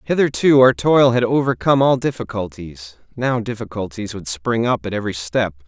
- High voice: No, low, 110 Hz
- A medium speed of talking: Yes, average, 160 wpm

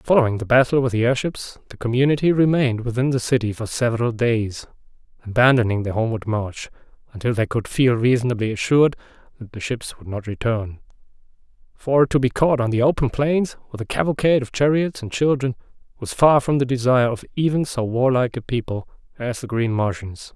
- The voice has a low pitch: Yes, low, 125 Hz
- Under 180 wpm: No, average, 185 wpm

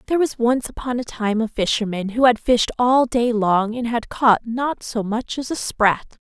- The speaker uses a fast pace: Yes, fast, 220 wpm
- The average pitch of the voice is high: Yes, high, 235 Hz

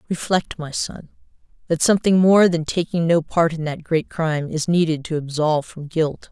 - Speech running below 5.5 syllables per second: Yes, 5.1 syllables/s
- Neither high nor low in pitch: Yes, medium, 160 Hz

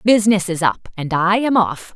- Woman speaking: Yes, female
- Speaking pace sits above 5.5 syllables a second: No, 5.1 syllables/s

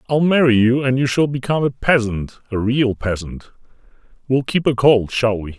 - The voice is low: Yes, low, 120 Hz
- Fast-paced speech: No, average, 195 wpm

